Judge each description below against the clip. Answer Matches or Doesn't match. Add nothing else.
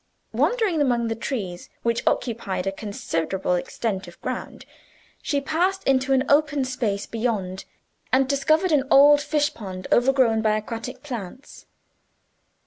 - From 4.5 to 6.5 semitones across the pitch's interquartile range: Matches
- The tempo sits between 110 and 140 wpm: Matches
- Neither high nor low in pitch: Doesn't match